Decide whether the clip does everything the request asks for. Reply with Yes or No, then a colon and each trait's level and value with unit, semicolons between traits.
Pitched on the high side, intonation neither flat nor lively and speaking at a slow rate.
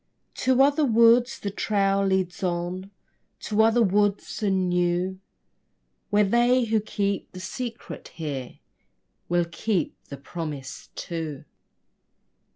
Yes: high, 195 Hz; average, 4.1 semitones; slow, 115 wpm